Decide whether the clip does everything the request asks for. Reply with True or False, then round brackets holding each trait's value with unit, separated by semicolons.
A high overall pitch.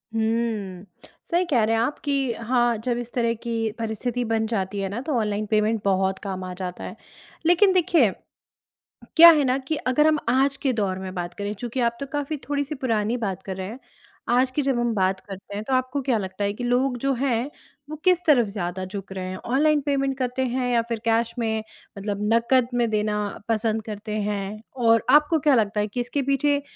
True (230 Hz)